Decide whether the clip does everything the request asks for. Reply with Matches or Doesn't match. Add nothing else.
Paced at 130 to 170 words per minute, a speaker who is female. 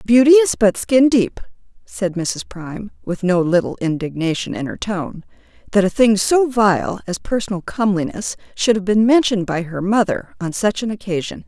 Doesn't match